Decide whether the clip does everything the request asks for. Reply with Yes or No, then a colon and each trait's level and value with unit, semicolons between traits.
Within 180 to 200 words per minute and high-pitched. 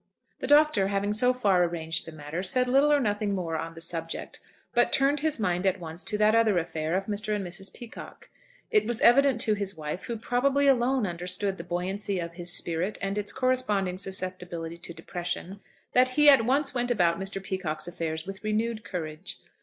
Yes: average, 195 wpm; high, 195 Hz